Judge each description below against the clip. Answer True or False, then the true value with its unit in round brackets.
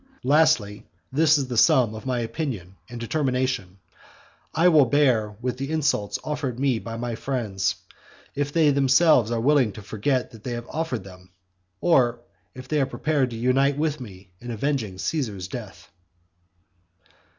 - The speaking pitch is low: True (125 Hz)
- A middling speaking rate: True (160 wpm)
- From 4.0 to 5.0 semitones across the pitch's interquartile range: True (4.6 semitones)